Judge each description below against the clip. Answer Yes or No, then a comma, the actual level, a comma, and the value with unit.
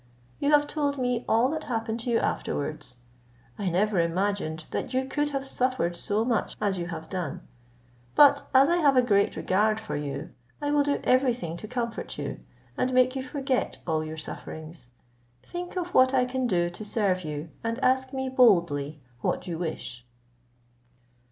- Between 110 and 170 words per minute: No, average, 180 wpm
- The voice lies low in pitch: No, high, 230 Hz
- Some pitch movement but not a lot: No, wide, 7.2 semitones